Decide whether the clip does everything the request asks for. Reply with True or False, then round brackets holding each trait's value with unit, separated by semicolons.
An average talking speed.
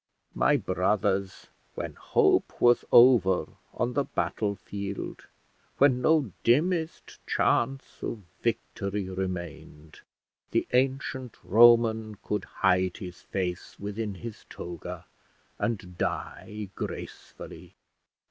False (100 wpm)